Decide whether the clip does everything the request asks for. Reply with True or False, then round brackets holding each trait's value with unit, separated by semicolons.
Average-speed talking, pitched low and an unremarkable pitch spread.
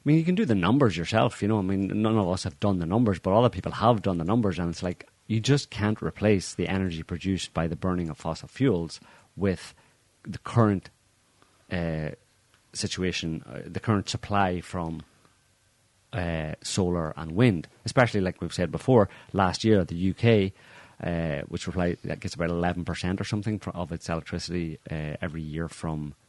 True (180 wpm; 95 Hz; 4.2 semitones)